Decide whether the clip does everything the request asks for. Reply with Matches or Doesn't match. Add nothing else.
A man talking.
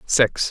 Matches